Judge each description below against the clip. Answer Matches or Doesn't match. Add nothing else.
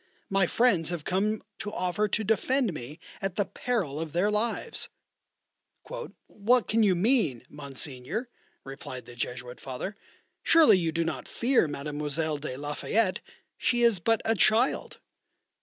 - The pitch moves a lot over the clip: Matches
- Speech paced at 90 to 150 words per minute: Matches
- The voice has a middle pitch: Matches